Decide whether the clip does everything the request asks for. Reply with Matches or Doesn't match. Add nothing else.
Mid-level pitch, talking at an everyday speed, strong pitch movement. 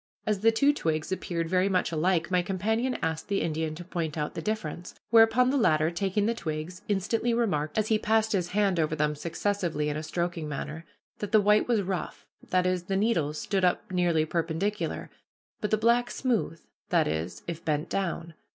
Doesn't match